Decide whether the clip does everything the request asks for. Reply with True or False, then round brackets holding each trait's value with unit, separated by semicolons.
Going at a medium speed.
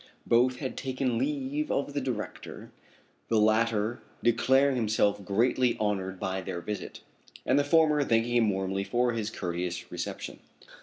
True (145 wpm)